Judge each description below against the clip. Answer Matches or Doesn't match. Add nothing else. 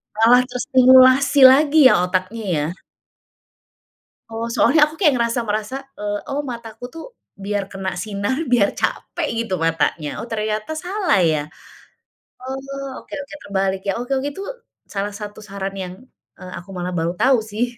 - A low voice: Doesn't match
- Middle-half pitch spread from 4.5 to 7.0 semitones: Matches